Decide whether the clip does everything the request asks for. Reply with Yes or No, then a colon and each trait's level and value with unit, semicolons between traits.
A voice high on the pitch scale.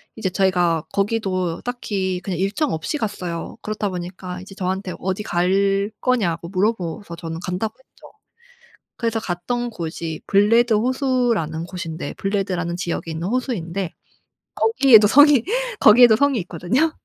Yes: high, 195 Hz